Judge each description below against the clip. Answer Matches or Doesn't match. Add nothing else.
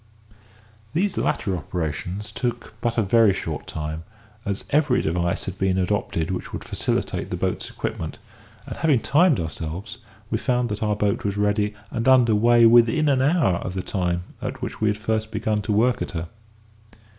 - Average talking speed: Matches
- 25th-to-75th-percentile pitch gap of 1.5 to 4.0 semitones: Doesn't match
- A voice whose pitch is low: Matches